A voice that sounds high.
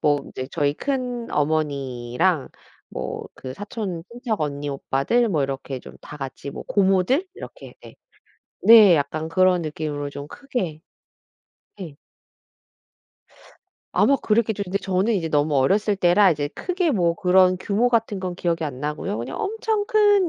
No: medium, 180 Hz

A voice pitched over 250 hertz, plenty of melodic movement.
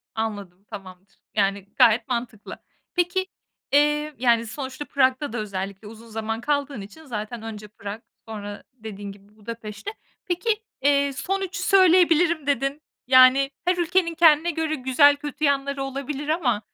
Yes: very high, 260 Hz; wide, 5.9 semitones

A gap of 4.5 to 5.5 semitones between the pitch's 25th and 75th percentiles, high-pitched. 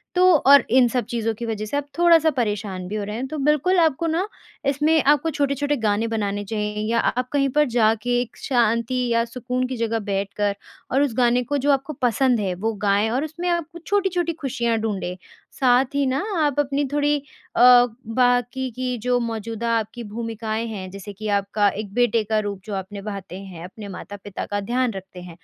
Yes: average, 4.8 semitones; high, 235 Hz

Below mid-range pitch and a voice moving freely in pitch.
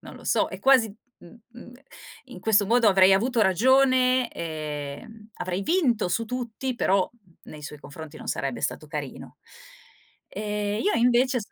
No: high, 210 Hz; wide, 6.0 semitones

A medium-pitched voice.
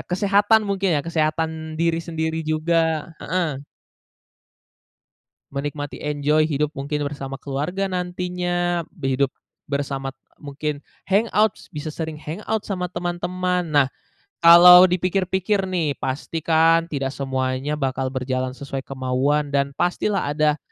Yes: medium, 155 Hz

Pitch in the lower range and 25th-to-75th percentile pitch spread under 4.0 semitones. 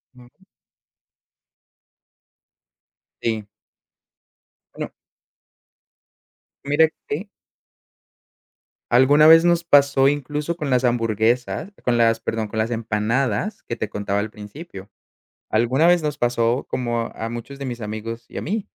No: low, 120 Hz; average, 4.4 semitones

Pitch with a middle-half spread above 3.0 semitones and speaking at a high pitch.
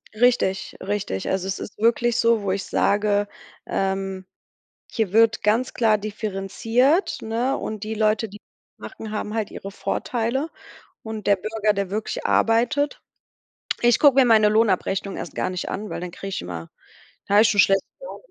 No: narrow, 2.6 semitones; high, 215 Hz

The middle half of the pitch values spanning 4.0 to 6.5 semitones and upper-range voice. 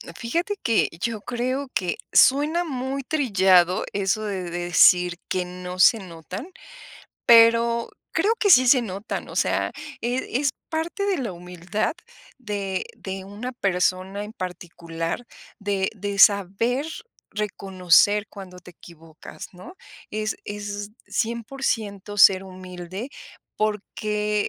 Yes: average, 4.5 semitones; high, 205 Hz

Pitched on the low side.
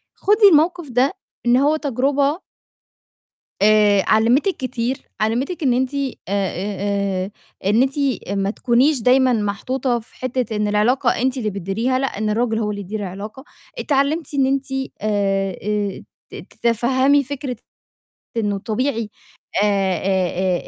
No: high, 240 Hz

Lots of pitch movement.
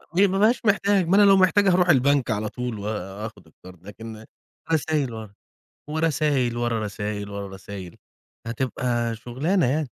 Yes: wide, 7.4 semitones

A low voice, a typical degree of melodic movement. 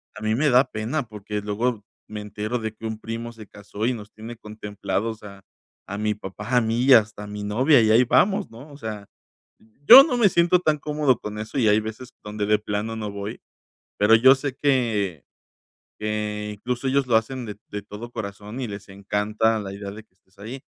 Yes: low, 110 Hz; average, 3.2 semitones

